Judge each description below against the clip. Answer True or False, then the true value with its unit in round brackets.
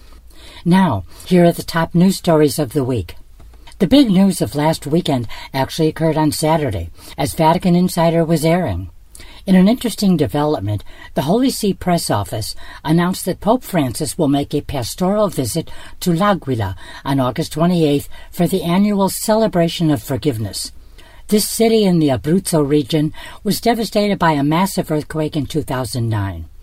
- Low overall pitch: False (160 Hz)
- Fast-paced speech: False (155 wpm)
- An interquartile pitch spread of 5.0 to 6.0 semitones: True (5.4 semitones)